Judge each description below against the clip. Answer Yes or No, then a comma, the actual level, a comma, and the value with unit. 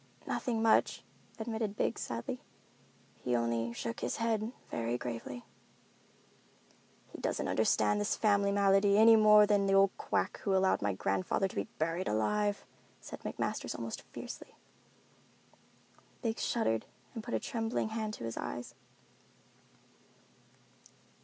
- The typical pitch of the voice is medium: No, high, 195 Hz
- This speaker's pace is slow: Yes, slow, 130 wpm